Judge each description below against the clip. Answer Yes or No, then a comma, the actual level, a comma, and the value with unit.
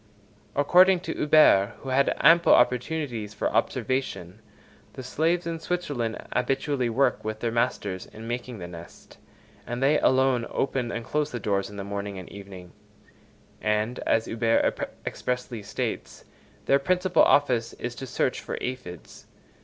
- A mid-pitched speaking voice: No, low, 125 Hz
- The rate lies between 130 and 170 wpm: Yes, average, 145 wpm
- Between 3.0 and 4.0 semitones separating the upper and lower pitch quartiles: No, average, 4.6 semitones